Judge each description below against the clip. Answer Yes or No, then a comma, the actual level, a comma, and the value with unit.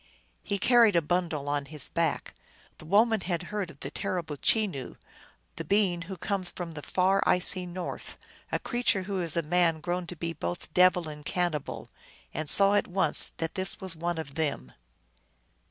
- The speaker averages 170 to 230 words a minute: Yes, average, 180 wpm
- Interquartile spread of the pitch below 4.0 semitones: Yes, average, 3.1 semitones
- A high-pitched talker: No, medium, 175 Hz